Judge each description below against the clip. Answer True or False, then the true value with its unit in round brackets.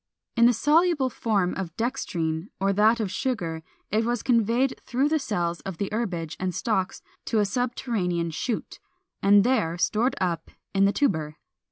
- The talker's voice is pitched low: False (210 Hz)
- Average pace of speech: True (165 wpm)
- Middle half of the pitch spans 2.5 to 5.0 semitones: False (5.4 semitones)